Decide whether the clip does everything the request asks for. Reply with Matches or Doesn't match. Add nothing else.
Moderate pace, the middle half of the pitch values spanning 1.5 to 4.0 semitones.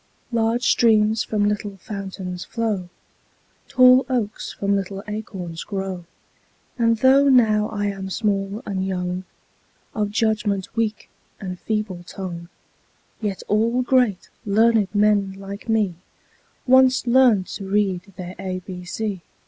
Doesn't match